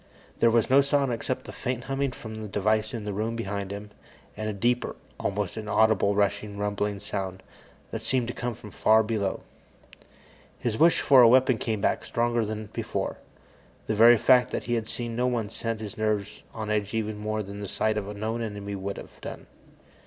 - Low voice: Yes, low, 110 Hz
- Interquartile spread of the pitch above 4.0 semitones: No, narrow, 2.4 semitones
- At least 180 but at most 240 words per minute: Yes, average, 200 wpm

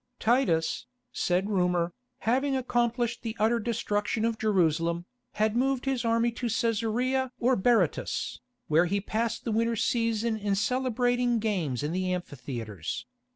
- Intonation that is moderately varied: Yes, average, 4.6 semitones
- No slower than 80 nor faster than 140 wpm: Yes, slow, 135 wpm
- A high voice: Yes, high, 225 Hz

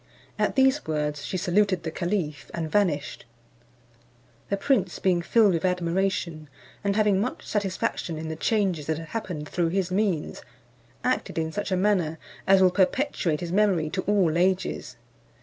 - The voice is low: No, medium, 185 Hz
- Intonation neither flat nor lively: Yes, average, 3.8 semitones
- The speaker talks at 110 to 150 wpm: No, average, 160 wpm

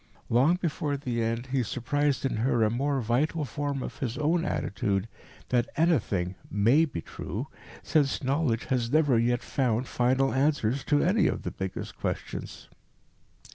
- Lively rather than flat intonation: No, average, 3.9 semitones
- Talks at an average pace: Yes, average, 155 wpm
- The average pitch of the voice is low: Yes, low, 130 Hz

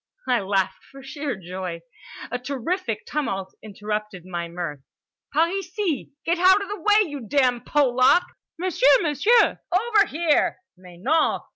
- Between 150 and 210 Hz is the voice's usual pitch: No, very high, 275 Hz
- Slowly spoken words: Yes, slow, 120 wpm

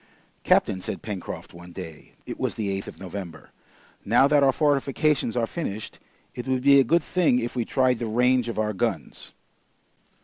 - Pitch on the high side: No, low, 120 Hz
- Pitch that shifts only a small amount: No, average, 5.1 semitones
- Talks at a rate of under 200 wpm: Yes, average, 180 wpm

